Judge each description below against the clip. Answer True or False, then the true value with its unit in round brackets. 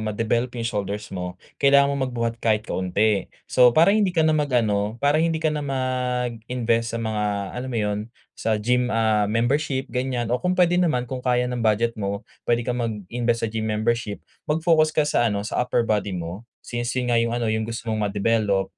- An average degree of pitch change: True (3.0 semitones)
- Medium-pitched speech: False (115 Hz)